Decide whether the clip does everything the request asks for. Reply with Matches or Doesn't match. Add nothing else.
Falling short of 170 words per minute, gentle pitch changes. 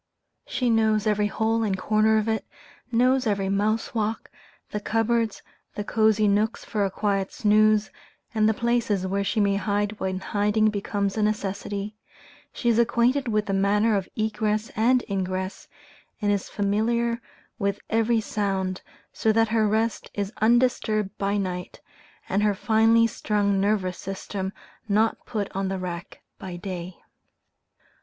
Matches